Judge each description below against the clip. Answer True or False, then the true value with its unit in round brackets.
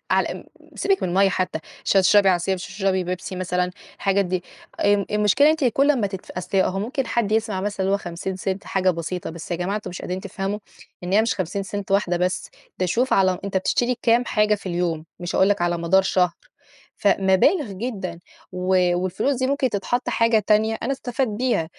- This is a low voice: False (195 Hz)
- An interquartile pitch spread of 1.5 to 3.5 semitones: True (3.1 semitones)